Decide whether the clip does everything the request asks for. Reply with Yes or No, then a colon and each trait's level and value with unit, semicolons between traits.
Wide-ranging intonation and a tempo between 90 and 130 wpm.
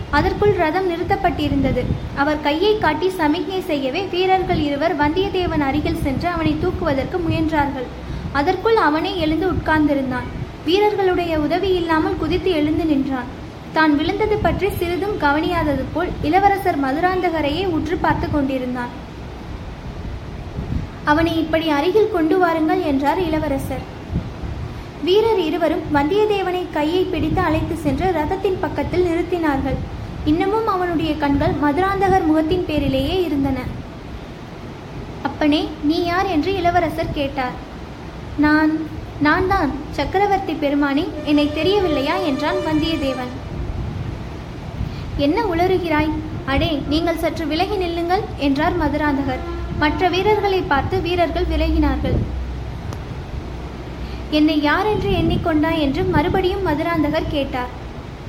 No: average, 3.6 semitones; average, 100 wpm